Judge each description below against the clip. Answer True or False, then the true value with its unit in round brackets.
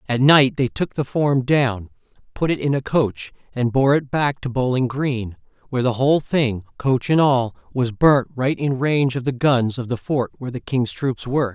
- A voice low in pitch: True (130 Hz)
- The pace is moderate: False (215 wpm)